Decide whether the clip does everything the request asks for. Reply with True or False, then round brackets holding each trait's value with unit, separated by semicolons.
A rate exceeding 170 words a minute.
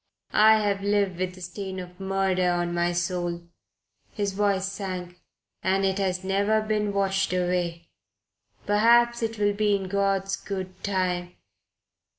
False (145 wpm)